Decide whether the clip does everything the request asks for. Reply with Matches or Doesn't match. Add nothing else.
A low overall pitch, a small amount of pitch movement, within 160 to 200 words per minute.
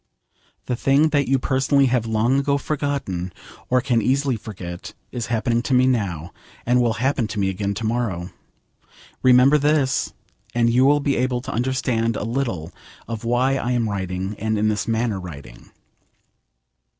Doesn't match